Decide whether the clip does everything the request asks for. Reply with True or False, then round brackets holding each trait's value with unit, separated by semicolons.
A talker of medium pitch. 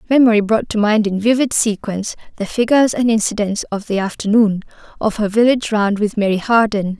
False (215 Hz)